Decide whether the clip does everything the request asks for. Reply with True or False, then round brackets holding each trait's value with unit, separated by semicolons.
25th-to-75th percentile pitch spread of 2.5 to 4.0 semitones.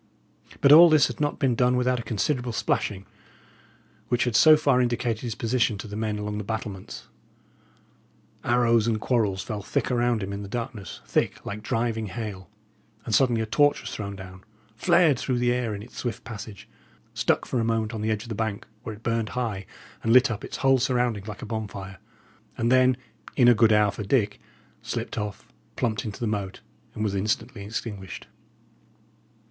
True (2.9 semitones)